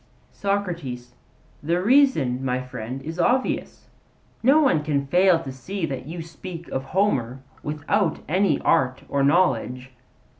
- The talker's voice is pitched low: No, medium, 155 Hz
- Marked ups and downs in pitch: Yes, wide, 6.0 semitones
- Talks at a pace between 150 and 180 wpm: No, slow, 135 wpm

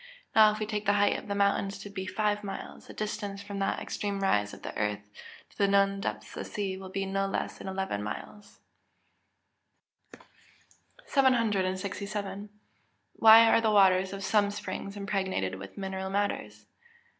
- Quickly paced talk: No, average, 170 wpm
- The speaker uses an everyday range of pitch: No, narrow, 1.4 semitones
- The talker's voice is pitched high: Yes, high, 200 Hz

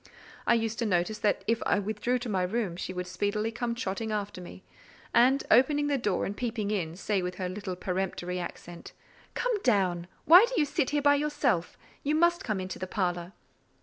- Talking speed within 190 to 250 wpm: Yes, average, 195 wpm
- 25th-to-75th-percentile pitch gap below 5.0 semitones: No, average, 5.3 semitones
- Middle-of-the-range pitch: No, high, 210 Hz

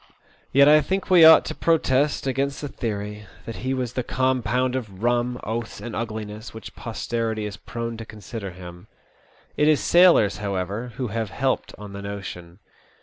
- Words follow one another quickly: No, average, 170 wpm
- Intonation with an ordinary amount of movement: Yes, average, 4.0 semitones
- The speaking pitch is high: No, low, 115 Hz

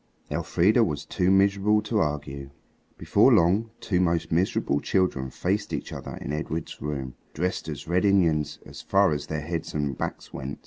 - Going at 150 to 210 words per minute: Yes, average, 170 wpm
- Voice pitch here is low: Yes, very low, 85 Hz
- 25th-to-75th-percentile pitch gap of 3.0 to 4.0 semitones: No, average, 4.7 semitones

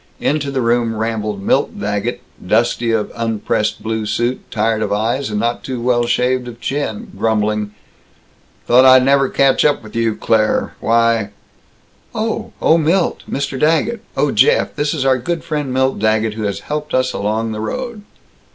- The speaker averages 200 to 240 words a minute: No, average, 170 wpm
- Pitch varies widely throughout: No, average, 3.9 semitones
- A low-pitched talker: Yes, low, 120 Hz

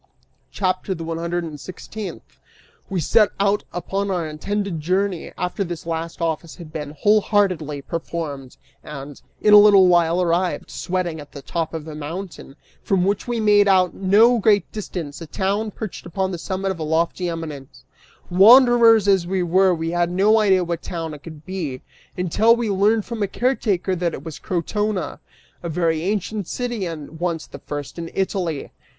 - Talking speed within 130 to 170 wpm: No, average, 180 wpm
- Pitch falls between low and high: Yes, medium, 180 Hz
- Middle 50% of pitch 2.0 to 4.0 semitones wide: Yes, average, 3.5 semitones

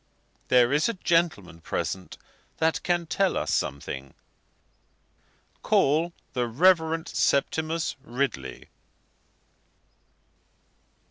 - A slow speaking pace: Yes, slow, 80 wpm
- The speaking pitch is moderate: Yes, medium, 150 Hz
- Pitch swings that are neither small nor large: No, wide, 6.0 semitones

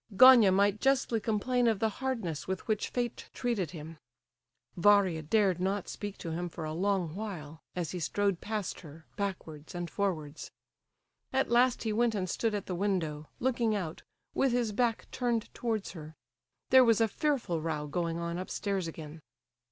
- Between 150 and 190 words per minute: Yes, average, 170 wpm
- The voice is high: Yes, high, 200 Hz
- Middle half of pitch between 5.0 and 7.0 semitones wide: Yes, average, 5.3 semitones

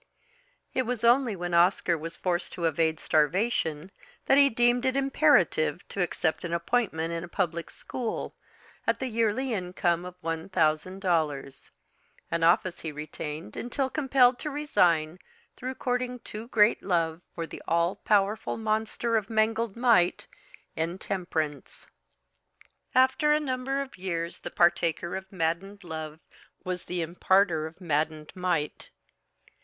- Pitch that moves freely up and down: Yes, wide, 6.1 semitones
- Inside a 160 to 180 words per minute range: No, average, 140 wpm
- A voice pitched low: No, medium, 180 Hz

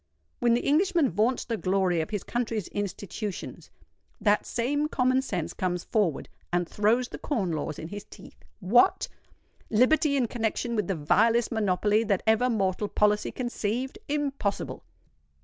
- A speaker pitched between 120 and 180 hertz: No, high, 215 Hz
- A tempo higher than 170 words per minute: No, average, 150 wpm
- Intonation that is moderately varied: Yes, average, 4.2 semitones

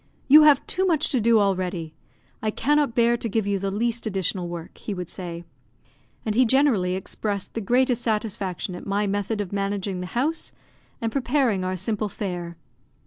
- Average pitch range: Yes, average, 4.2 semitones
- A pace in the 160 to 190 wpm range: Yes, average, 180 wpm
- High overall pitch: Yes, high, 205 Hz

